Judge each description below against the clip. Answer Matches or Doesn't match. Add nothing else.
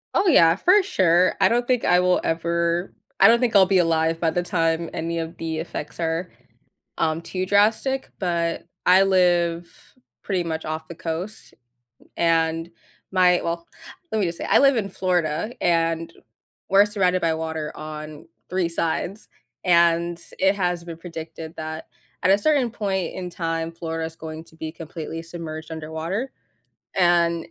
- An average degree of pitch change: Doesn't match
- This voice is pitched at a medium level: Matches